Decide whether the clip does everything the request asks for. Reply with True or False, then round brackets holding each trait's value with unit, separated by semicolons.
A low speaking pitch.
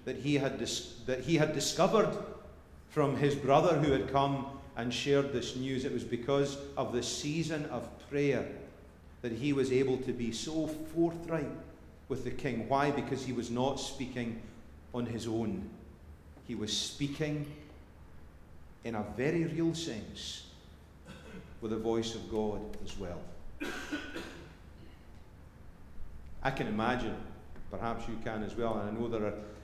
True (115 Hz)